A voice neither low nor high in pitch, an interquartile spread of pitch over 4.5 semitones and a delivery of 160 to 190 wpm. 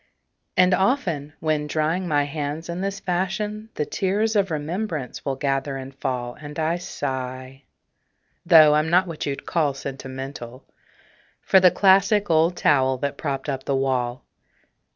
No: medium, 150 Hz; average, 5.1 semitones; average, 150 wpm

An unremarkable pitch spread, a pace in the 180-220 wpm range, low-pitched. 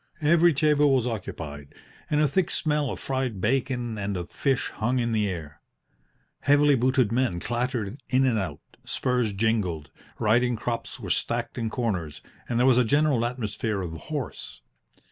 No: average, 4.3 semitones; average, 165 wpm; low, 120 Hz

